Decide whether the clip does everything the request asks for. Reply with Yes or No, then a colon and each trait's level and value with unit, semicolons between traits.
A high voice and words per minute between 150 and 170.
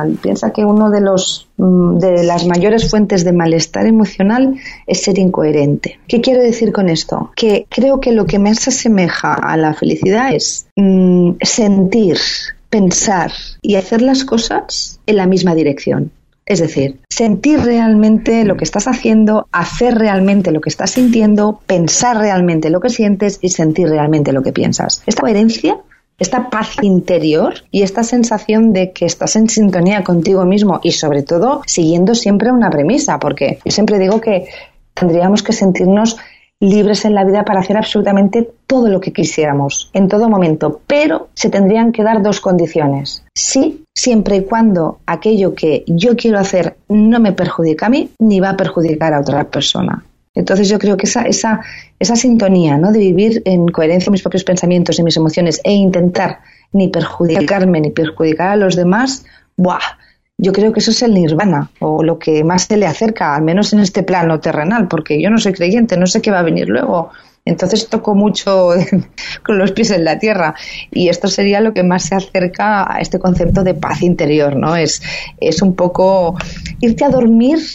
No: high, 195 Hz; average, 180 wpm